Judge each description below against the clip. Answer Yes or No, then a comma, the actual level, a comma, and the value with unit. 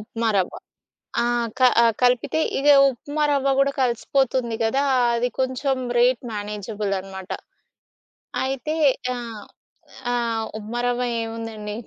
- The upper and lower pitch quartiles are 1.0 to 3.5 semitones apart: Yes, average, 2.9 semitones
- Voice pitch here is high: Yes, high, 235 Hz